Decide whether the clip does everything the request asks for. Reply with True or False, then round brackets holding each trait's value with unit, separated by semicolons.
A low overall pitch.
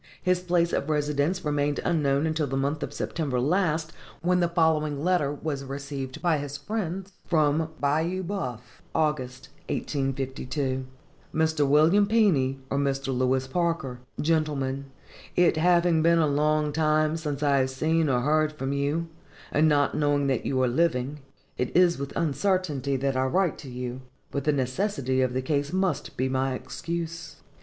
False (150 Hz)